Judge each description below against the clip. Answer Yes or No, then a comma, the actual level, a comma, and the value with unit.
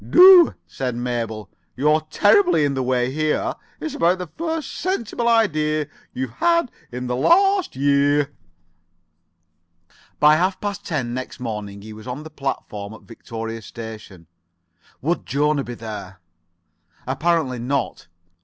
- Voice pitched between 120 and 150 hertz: Yes, medium, 140 Hz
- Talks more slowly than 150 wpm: Yes, slow, 135 wpm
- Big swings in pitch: Yes, wide, 6.3 semitones